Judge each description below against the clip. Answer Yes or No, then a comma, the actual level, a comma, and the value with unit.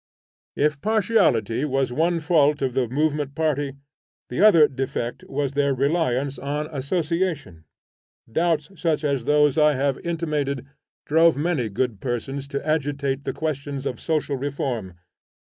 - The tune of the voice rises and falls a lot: No, average, 2.7 semitones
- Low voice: No, medium, 145 Hz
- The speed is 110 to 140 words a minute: Yes, slow, 135 wpm